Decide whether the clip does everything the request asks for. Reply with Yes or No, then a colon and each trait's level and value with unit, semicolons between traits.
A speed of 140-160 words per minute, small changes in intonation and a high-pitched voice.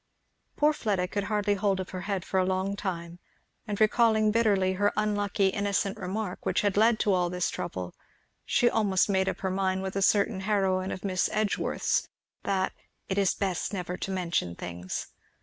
No: average, 185 wpm; narrow, 1.8 semitones; high, 195 Hz